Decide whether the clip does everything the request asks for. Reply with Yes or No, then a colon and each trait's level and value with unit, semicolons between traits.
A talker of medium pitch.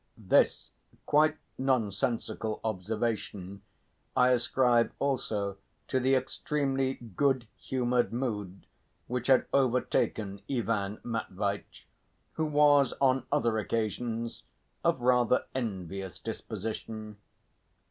No: low, 120 Hz